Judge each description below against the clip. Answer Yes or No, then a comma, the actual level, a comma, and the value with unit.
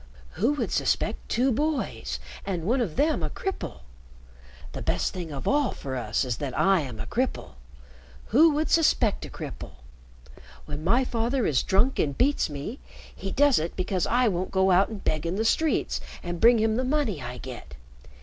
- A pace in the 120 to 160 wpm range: No, average, 190 wpm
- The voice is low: No, high, 200 Hz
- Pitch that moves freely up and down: Yes, wide, 8.7 semitones